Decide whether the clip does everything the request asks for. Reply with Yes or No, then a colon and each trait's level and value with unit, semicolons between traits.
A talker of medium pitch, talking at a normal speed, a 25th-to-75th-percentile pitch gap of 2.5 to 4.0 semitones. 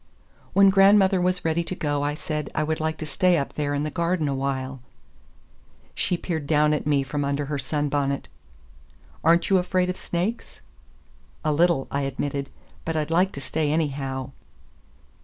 Yes: medium, 150 Hz; average, 175 wpm; average, 3.4 semitones